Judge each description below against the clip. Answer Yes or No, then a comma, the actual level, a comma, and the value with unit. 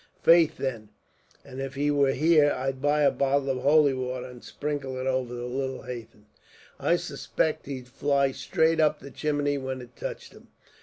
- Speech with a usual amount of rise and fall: No, narrow, 2.2 semitones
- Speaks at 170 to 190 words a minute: Yes, average, 185 wpm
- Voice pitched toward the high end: No, low, 135 Hz